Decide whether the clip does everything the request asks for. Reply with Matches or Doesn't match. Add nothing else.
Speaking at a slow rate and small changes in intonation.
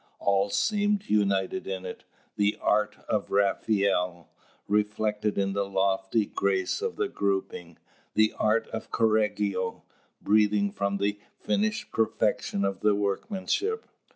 Matches